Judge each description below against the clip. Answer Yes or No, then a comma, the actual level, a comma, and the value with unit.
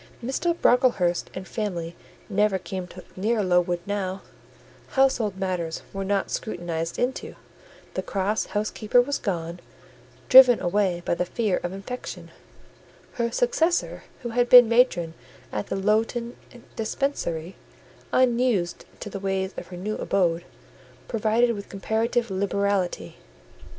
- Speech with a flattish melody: No, average, 4.6 semitones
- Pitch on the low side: No, high, 200 Hz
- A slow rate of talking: Yes, slow, 125 wpm